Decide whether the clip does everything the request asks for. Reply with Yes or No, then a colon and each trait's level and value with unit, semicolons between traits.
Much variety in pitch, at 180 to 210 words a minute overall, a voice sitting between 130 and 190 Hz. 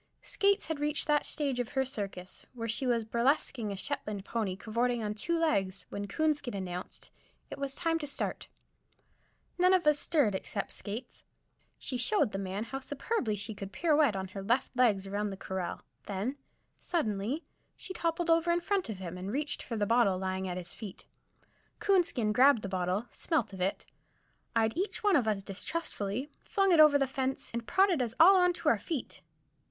No: wide, 7.3 semitones; average, 190 wpm; high, 240 Hz